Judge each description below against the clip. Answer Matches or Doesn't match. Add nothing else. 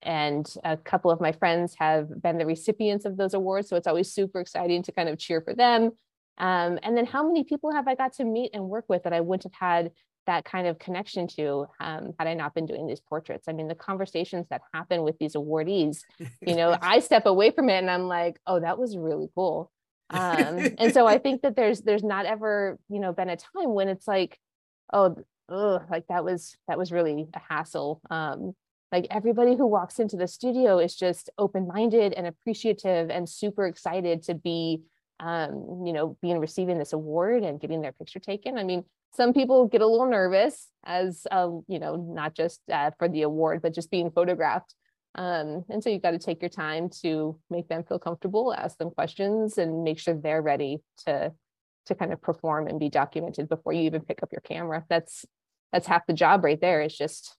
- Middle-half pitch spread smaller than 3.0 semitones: Doesn't match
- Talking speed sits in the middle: Doesn't match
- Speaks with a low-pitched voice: Doesn't match